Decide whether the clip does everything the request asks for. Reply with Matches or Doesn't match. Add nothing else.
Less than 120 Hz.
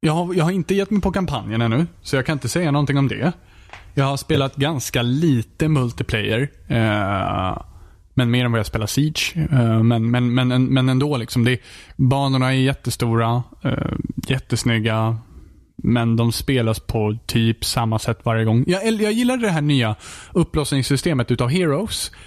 Doesn't match